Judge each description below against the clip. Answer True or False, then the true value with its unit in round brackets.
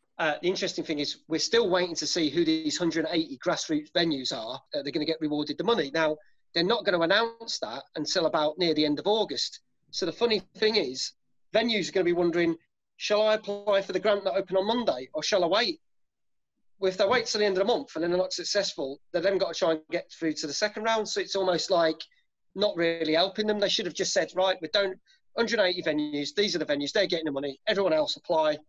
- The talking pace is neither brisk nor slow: False (250 wpm)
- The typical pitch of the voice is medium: True (180 Hz)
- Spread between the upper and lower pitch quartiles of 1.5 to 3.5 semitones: False (4.8 semitones)